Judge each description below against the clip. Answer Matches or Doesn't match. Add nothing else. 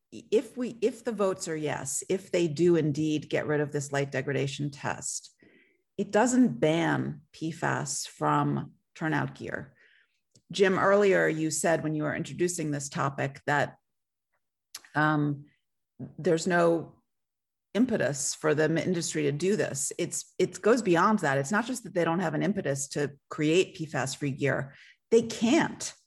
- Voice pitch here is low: Doesn't match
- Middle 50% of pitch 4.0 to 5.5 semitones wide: Matches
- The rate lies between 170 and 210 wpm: Doesn't match